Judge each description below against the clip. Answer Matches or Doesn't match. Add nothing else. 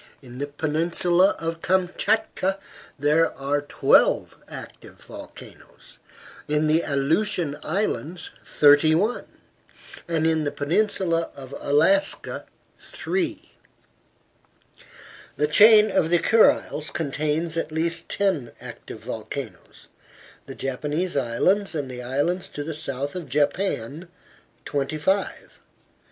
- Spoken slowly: Matches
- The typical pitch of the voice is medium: Matches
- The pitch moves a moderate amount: Matches